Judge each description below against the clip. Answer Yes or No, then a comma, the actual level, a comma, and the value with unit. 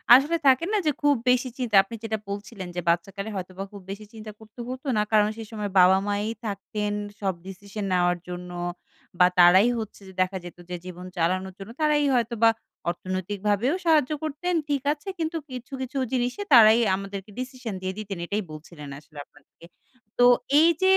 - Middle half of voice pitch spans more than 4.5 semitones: Yes, average, 5.1 semitones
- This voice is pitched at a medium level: No, high, 210 Hz